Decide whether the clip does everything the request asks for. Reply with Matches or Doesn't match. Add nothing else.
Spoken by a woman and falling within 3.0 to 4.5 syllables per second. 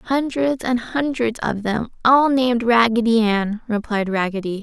Matches